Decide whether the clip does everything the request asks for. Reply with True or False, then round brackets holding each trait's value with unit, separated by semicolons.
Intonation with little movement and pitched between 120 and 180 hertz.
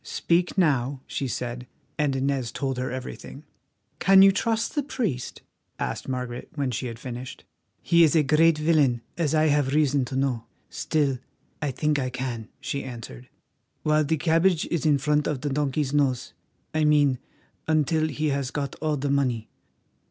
False (3.3 semitones; 140 Hz)